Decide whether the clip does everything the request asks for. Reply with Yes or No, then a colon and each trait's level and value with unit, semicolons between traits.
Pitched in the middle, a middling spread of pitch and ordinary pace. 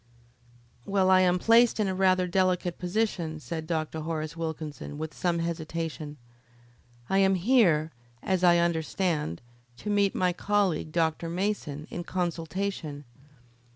No: medium, 175 Hz; average, 3.1 semitones; slow, 130 wpm